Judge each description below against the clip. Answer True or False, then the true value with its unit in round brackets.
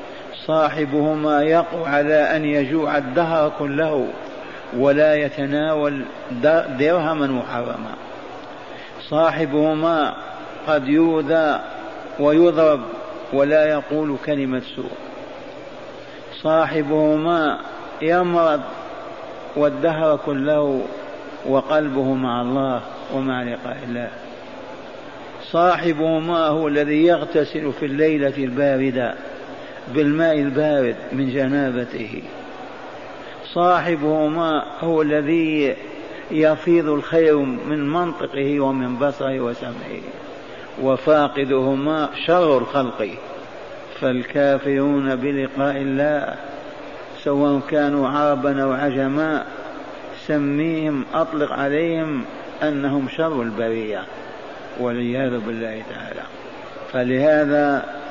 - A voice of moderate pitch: True (150 Hz)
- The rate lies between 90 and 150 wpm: False (75 wpm)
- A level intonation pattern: True (2.3 semitones)